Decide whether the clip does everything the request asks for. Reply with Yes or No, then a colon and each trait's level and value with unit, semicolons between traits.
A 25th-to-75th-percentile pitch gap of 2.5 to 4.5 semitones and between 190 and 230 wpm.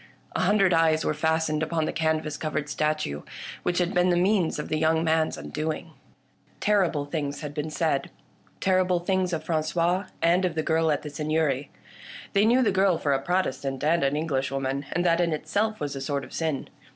Yes: average, 2.9 semitones; average, 200 wpm